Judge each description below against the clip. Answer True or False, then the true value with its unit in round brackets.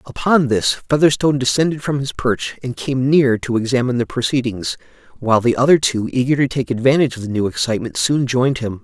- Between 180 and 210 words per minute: True (195 wpm)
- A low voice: True (130 Hz)